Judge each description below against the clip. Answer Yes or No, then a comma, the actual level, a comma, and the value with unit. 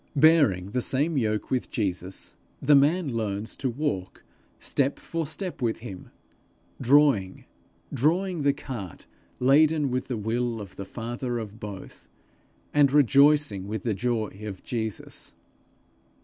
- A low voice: Yes, low, 125 Hz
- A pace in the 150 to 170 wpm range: No, slow, 135 wpm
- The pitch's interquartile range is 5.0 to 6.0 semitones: Yes, wide, 5.4 semitones